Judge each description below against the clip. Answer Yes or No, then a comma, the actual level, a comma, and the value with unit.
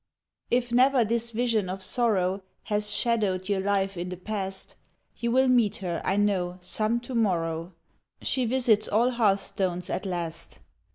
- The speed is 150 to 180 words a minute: Yes, average, 155 wpm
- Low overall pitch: No, high, 205 Hz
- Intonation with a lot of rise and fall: No, average, 4.1 semitones